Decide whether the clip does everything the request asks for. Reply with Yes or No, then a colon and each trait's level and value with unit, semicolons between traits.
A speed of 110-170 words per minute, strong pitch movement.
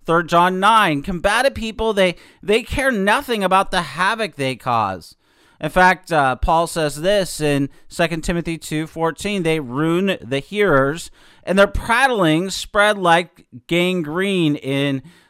No: average, 140 wpm; average, 3.8 semitones